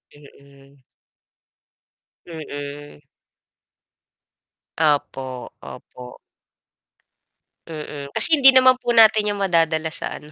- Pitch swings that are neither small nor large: No, wide, 6.4 semitones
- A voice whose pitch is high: No, medium, 155 Hz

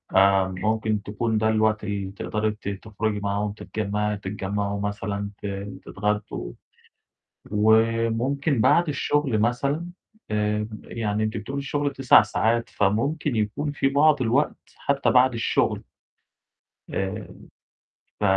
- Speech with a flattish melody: No, average, 3.4 semitones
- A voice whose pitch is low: Yes, low, 110 Hz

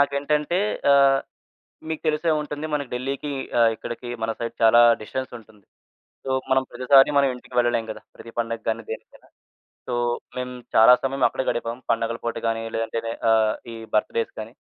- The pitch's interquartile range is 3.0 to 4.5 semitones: Yes, average, 3.3 semitones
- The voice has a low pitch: Yes, low, 120 Hz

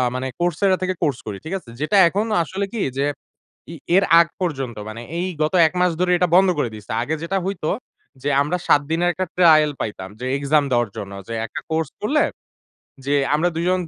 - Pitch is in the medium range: Yes, medium, 160 Hz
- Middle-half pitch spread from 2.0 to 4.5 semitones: No, average, 5.0 semitones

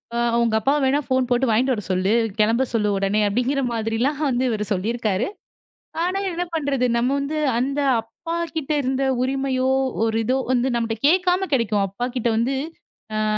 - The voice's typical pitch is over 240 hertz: Yes, very high, 250 Hz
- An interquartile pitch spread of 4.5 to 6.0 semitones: No, average, 3.5 semitones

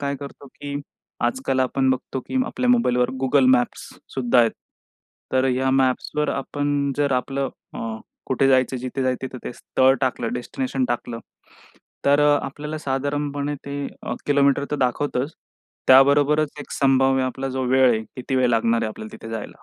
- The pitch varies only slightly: Yes, narrow, 1.9 semitones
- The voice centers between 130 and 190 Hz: Yes, low, 135 Hz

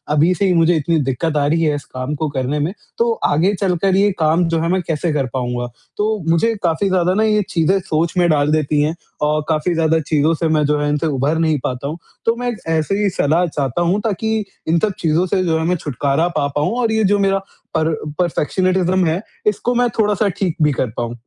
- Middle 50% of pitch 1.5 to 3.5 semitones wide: No, average, 4.0 semitones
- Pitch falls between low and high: Yes, medium, 165 Hz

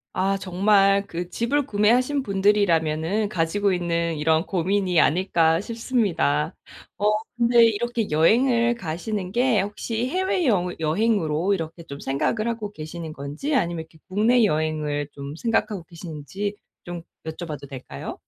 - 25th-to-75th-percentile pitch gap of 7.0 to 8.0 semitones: No, wide, 5.5 semitones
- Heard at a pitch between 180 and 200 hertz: Yes, high, 190 Hz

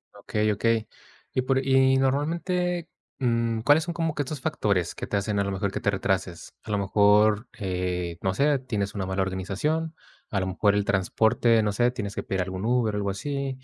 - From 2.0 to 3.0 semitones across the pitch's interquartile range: No, average, 5.3 semitones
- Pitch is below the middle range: Yes, low, 110 Hz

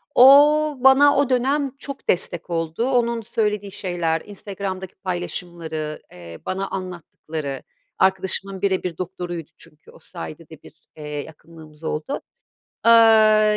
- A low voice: No, high, 190 Hz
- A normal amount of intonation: No, wide, 5.8 semitones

